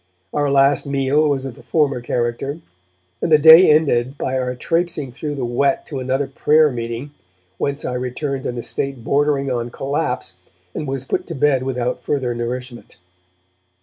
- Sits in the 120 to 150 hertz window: Yes, low, 135 Hz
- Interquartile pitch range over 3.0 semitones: No, average, 2.7 semitones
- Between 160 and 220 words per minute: Yes, average, 170 wpm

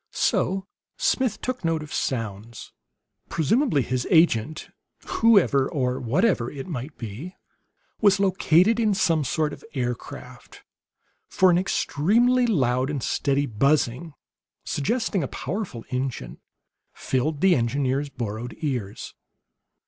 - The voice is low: No, medium, 145 Hz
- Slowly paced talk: Yes, slow, 115 wpm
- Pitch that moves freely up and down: Yes, wide, 6.9 semitones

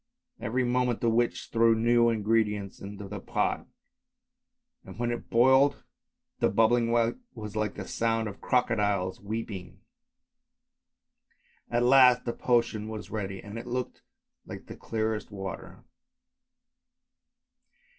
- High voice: No, low, 115 Hz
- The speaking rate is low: Yes, slow, 120 wpm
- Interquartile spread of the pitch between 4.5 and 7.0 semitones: No, narrow, 2.6 semitones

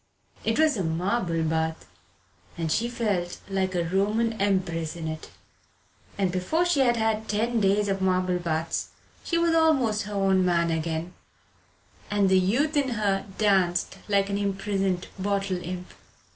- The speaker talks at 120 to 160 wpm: Yes, average, 155 wpm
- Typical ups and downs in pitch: Yes, average, 3.5 semitones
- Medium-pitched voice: No, high, 195 Hz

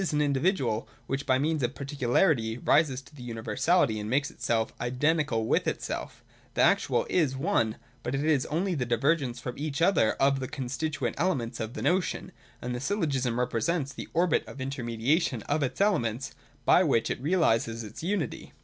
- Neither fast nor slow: Yes, average, 175 wpm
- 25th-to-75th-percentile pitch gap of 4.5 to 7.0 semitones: Yes, average, 4.8 semitones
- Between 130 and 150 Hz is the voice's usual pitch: Yes, low, 135 Hz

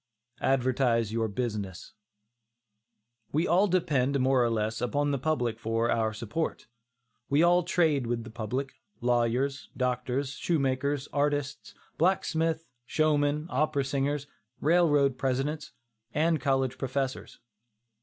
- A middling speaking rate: No, slow, 115 wpm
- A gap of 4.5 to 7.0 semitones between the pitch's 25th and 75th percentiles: No, average, 3.5 semitones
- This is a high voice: No, low, 135 Hz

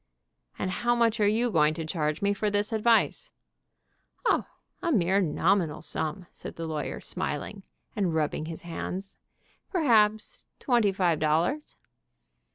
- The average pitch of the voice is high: Yes, high, 195 Hz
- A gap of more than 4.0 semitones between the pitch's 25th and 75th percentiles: Yes, average, 5.2 semitones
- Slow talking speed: No, average, 145 wpm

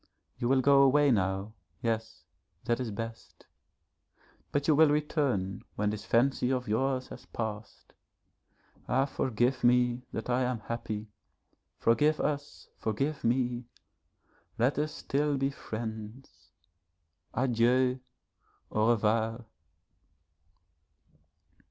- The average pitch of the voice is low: Yes, low, 120 Hz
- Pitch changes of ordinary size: Yes, average, 3.4 semitones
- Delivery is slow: Yes, slow, 110 wpm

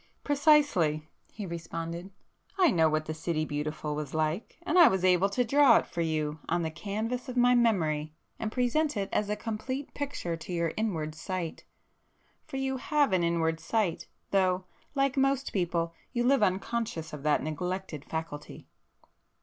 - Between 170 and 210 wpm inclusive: No, average, 160 wpm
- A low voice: No, medium, 185 Hz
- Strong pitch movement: Yes, wide, 7.2 semitones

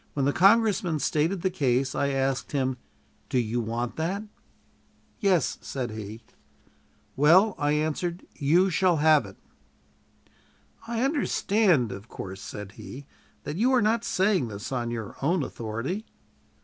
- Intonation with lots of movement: Yes, wide, 7.6 semitones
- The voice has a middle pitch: Yes, medium, 150 Hz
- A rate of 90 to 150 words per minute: Yes, average, 140 wpm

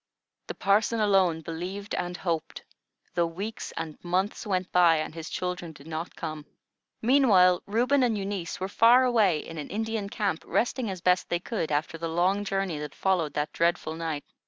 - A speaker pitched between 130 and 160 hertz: No, medium, 180 Hz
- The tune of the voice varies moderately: Yes, average, 3.8 semitones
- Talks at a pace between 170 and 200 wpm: Yes, average, 180 wpm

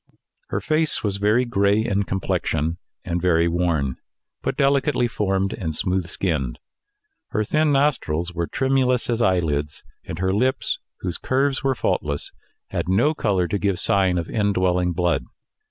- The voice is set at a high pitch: No, very low, 95 Hz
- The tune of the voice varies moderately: No, wide, 5.9 semitones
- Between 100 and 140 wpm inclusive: No, average, 150 wpm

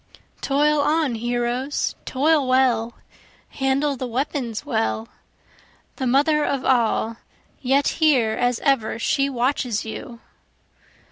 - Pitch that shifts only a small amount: No, average, 3.1 semitones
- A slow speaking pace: Yes, slow, 110 wpm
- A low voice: No, very high, 260 Hz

